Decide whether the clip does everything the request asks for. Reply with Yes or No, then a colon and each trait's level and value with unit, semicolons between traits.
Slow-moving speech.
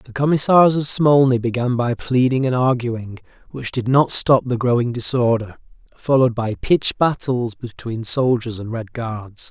No: average, 160 wpm